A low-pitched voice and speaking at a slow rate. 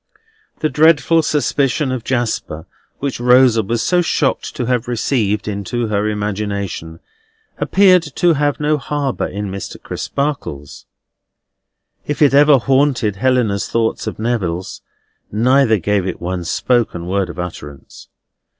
Yes: low, 120 Hz; slow, 130 wpm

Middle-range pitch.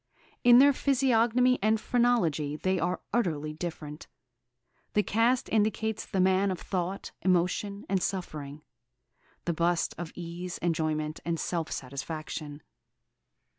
Yes: medium, 180 Hz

